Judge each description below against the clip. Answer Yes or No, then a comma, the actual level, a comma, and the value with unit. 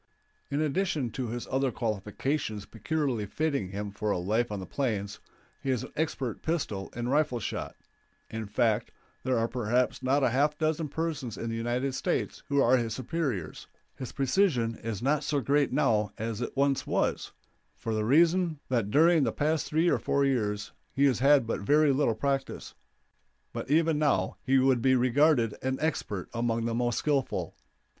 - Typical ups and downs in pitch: Yes, average, 4.4 semitones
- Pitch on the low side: Yes, low, 130 Hz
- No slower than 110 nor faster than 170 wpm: No, average, 180 wpm